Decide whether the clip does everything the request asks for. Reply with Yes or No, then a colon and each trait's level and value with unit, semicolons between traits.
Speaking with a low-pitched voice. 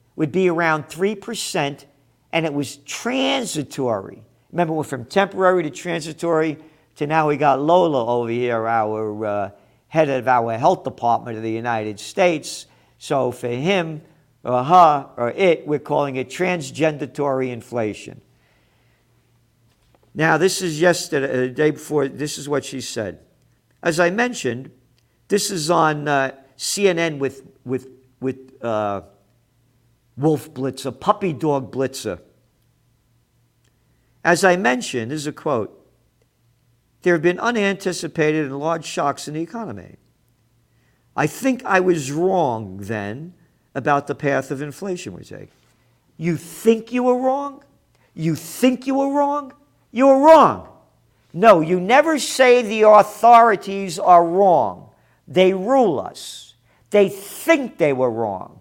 No: medium, 150 Hz